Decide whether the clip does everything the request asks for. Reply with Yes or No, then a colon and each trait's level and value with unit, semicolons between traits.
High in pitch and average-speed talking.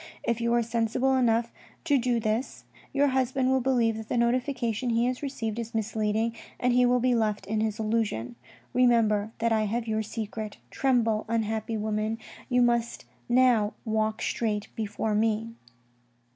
Yes: high, 230 Hz; average, 160 wpm